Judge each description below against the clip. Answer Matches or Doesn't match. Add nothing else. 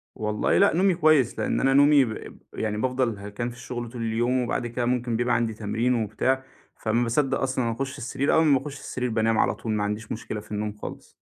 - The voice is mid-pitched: Doesn't match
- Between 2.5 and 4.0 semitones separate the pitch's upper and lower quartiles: Matches